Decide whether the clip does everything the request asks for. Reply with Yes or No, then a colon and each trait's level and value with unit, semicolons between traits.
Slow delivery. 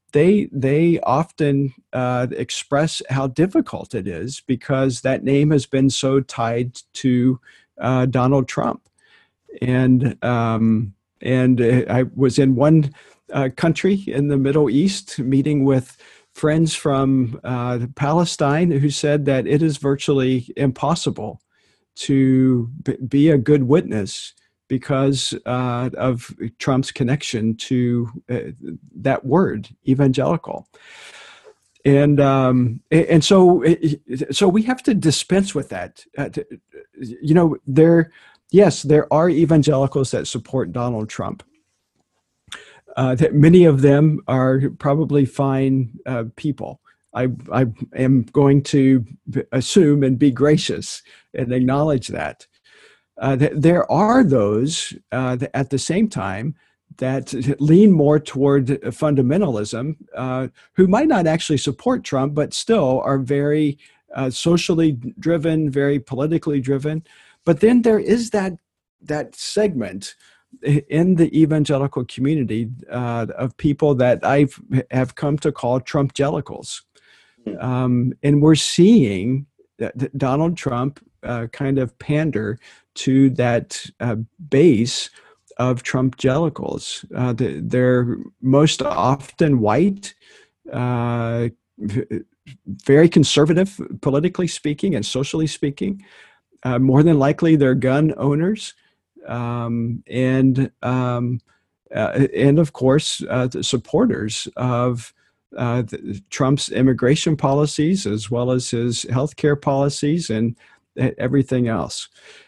Yes: slow, 120 wpm